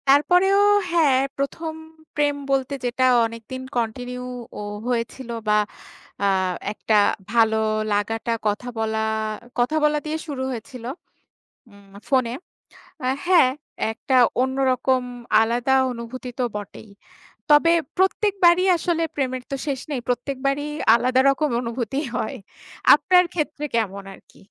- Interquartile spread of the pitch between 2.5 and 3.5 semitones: No, average, 4.1 semitones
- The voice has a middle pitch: No, very high, 255 Hz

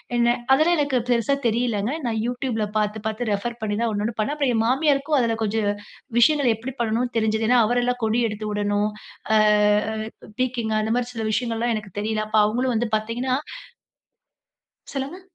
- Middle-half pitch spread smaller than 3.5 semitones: Yes, narrow, 2.5 semitones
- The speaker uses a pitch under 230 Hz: No, high, 235 Hz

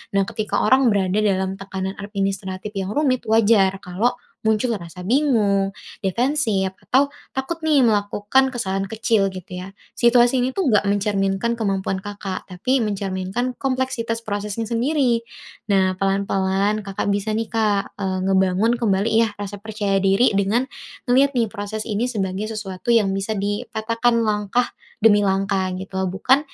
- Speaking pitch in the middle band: No, high, 205 Hz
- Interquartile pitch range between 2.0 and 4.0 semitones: Yes, average, 3.3 semitones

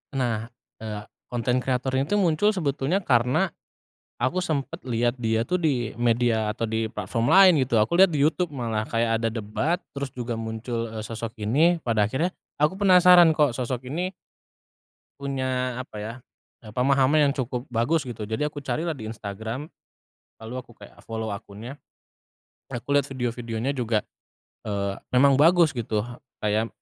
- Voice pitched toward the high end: No, low, 125 Hz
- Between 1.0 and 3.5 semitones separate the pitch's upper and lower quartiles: No, average, 4.5 semitones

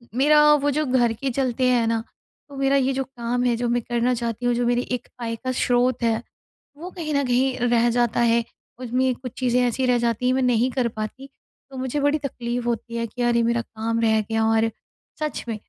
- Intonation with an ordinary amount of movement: No, narrow, 1.9 semitones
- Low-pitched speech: No, high, 245 Hz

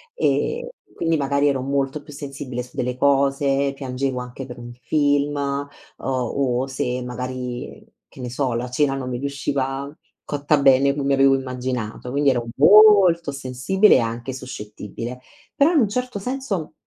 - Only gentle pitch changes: Yes, narrow, 2.3 semitones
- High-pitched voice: No, low, 135 Hz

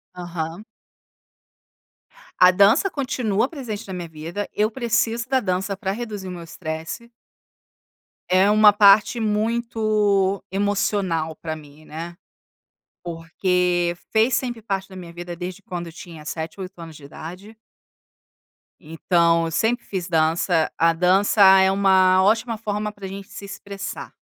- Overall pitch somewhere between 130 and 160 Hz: No, high, 190 Hz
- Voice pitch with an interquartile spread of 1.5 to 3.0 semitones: No, average, 3.7 semitones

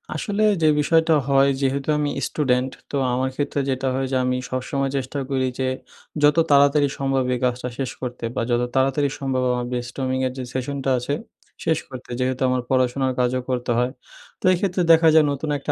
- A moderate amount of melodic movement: No, narrow, 1.9 semitones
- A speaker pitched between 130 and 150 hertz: Yes, low, 135 Hz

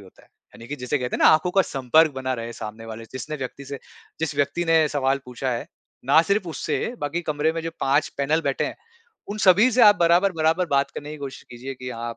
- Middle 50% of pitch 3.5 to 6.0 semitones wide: Yes, average, 4.1 semitones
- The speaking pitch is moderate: Yes, medium, 145 Hz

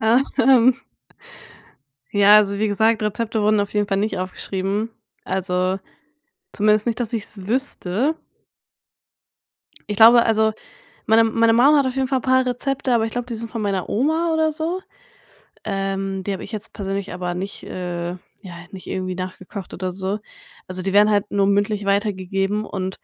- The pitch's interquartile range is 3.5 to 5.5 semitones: No, average, 3.1 semitones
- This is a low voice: No, high, 210 Hz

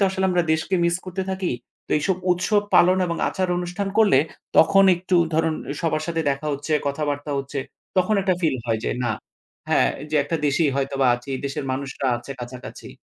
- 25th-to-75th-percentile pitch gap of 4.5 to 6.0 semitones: Yes, average, 4.9 semitones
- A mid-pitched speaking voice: Yes, medium, 160 Hz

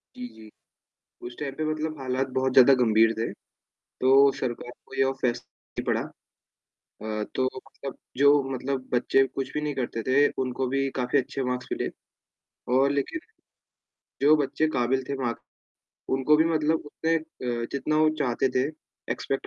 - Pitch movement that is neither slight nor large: No, narrow, 2.3 semitones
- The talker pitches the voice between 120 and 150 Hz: Yes, low, 135 Hz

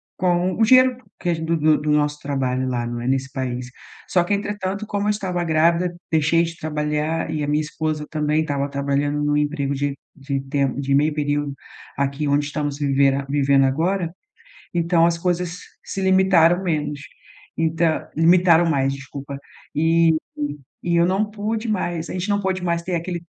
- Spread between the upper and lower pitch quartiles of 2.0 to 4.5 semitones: Yes, average, 3.7 semitones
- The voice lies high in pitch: No, medium, 155 Hz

